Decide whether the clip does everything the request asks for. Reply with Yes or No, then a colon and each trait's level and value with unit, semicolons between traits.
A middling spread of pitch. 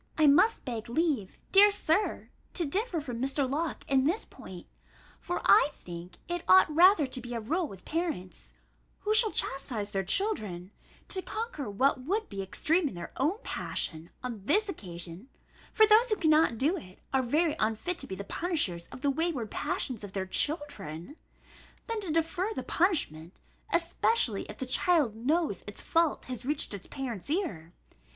No: wide, 9.0 semitones